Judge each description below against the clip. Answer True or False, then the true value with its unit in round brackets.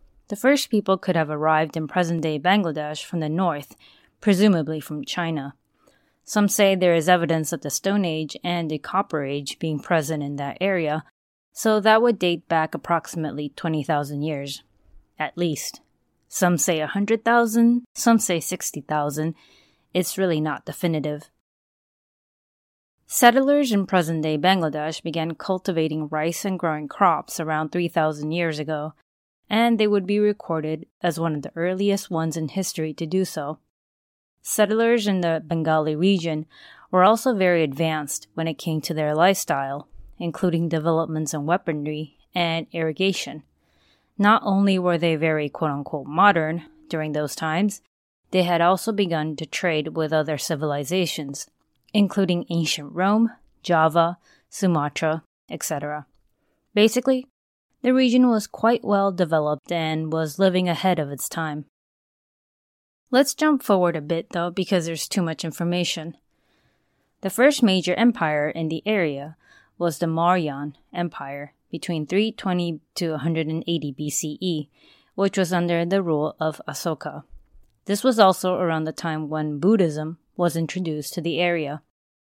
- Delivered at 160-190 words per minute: False (145 wpm)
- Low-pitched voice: False (165 Hz)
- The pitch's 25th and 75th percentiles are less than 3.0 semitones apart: False (3.5 semitones)